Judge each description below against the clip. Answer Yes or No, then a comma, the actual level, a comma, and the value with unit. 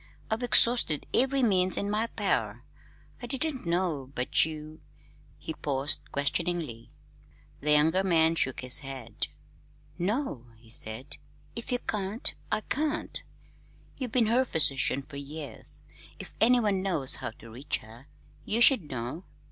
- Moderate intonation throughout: No, wide, 8.5 semitones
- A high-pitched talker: No, medium, 165 Hz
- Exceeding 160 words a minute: No, average, 140 wpm